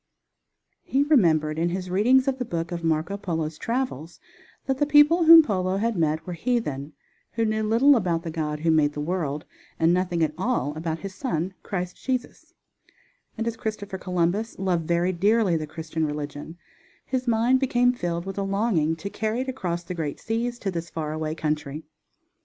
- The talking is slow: No, average, 185 wpm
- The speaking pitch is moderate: Yes, medium, 180 Hz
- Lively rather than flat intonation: Yes, wide, 6.0 semitones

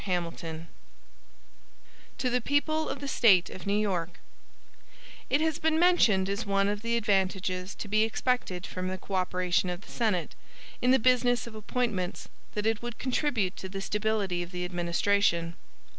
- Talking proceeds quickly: No, average, 165 wpm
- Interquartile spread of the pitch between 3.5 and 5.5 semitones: Yes, average, 4.7 semitones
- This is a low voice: No, high, 200 Hz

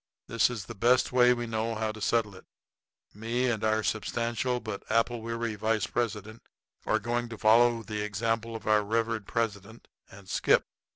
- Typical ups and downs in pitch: No, narrow, 1.6 semitones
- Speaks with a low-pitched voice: Yes, low, 115 Hz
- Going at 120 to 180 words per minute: Yes, average, 175 wpm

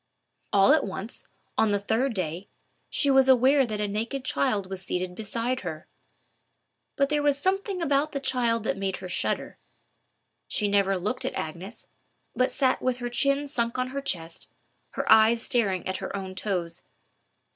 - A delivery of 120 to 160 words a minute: No, average, 175 wpm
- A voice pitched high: Yes, high, 230 Hz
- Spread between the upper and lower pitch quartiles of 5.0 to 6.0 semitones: Yes, wide, 5.6 semitones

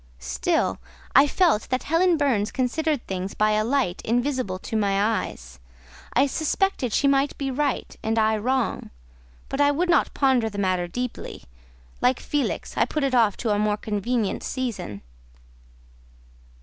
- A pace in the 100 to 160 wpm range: Yes, average, 155 wpm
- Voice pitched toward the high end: Yes, high, 245 Hz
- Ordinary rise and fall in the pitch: Yes, average, 5.0 semitones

